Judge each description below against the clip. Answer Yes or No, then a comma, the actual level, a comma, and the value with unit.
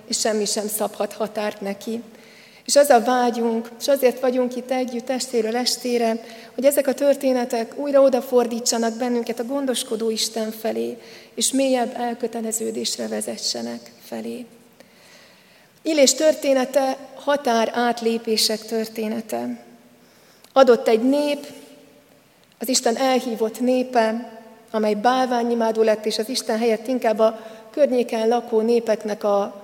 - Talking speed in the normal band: Yes, average, 115 wpm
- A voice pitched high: Yes, high, 230 Hz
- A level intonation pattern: Yes, narrow, 2.3 semitones